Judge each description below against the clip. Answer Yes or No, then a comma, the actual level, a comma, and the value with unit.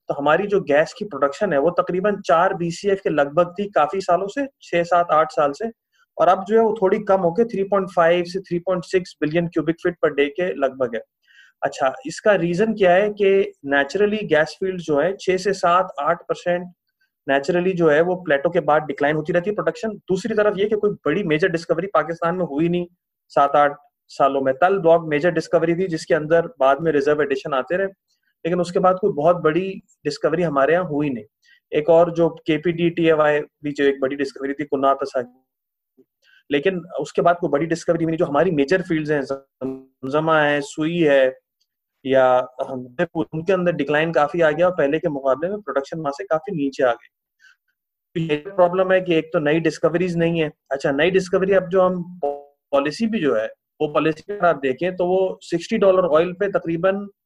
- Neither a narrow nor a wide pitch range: Yes, average, 4.2 semitones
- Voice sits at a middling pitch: Yes, medium, 170 Hz